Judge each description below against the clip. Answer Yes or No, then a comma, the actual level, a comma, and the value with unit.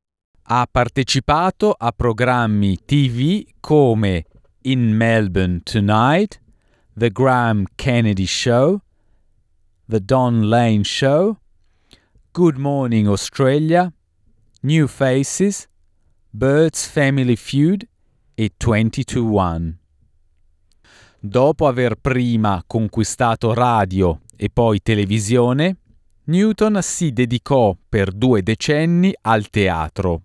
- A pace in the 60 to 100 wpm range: Yes, slow, 85 wpm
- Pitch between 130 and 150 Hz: No, low, 115 Hz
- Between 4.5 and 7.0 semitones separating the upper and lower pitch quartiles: Yes, average, 5.2 semitones